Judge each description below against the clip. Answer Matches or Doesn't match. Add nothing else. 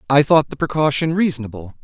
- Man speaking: Matches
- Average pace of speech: Matches